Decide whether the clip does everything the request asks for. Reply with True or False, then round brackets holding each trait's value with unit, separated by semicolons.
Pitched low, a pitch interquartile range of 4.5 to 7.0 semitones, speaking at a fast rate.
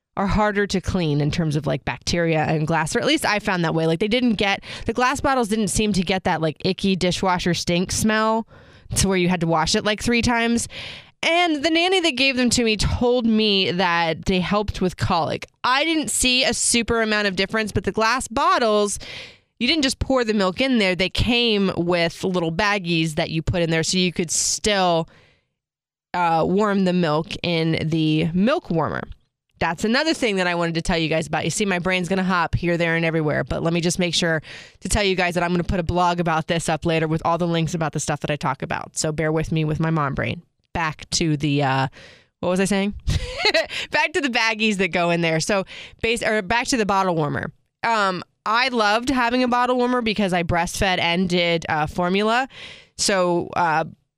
False (185 Hz; 5.0 semitones; 225 wpm)